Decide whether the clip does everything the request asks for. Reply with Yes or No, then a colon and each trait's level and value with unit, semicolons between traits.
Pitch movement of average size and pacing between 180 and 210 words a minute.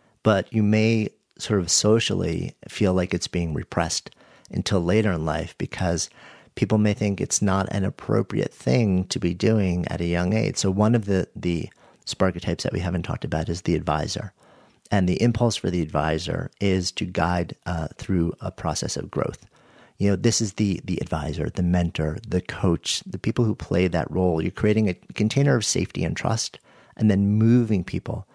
Yes: average, 3.6 semitones; average, 190 wpm